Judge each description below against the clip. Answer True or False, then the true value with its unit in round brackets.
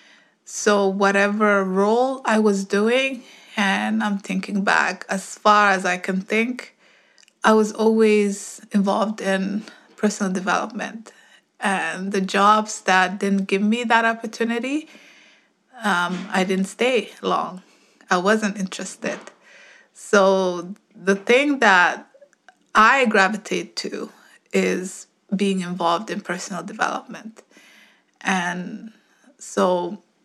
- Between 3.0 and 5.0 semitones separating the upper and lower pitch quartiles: False (2.5 semitones)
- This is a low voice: False (200 Hz)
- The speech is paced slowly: True (110 wpm)